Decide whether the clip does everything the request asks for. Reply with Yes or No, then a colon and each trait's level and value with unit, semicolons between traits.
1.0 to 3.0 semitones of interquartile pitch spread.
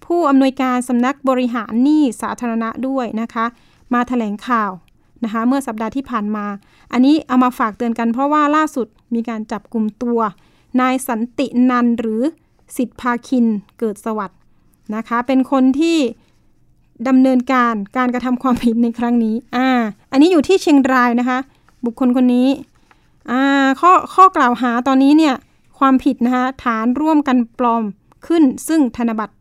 Yes: narrow, 2.5 semitones